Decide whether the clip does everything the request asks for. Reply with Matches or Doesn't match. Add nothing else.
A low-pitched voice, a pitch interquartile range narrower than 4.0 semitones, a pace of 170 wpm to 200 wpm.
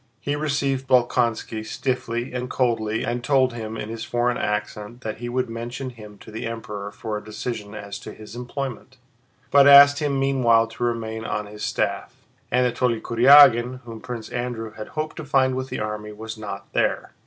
Matches